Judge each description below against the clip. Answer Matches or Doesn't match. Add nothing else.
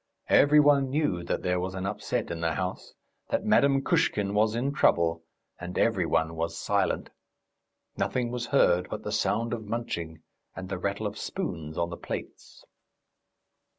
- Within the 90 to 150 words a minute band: Doesn't match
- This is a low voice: Matches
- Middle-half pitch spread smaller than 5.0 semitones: Doesn't match